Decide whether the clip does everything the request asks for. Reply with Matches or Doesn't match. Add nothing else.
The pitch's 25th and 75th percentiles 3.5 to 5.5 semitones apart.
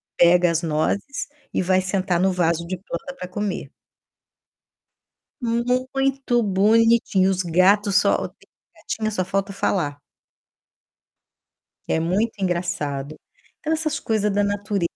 Matches